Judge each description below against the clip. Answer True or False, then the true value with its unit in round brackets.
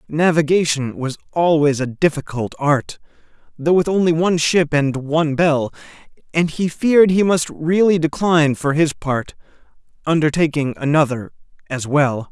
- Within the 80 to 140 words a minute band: True (135 wpm)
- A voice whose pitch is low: False (155 Hz)